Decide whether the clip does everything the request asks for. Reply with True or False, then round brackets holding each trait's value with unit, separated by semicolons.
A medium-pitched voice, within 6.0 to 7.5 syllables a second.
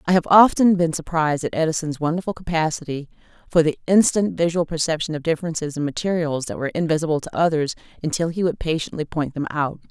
True (160 Hz; 6.5 syllables/s)